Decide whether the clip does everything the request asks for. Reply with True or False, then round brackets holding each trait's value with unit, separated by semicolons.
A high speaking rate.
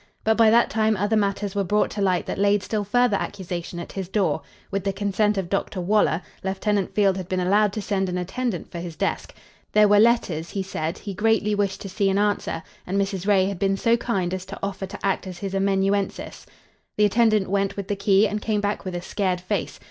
True (230 wpm)